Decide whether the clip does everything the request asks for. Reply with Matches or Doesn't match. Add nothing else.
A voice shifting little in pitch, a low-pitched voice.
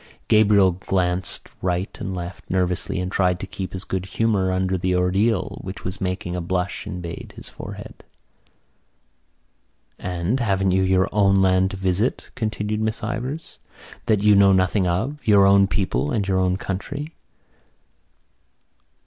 Matches